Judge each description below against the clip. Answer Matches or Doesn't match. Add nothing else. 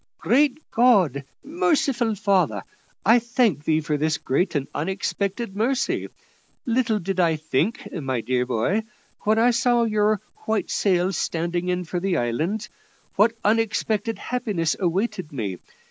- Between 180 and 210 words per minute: Doesn't match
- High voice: Matches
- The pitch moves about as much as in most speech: Doesn't match